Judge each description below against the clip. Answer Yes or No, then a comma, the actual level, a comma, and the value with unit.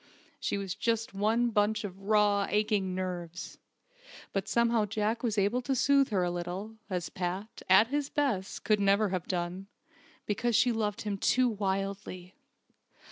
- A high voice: Yes, high, 205 Hz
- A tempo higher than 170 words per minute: No, average, 155 wpm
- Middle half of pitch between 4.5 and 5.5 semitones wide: No, average, 2.9 semitones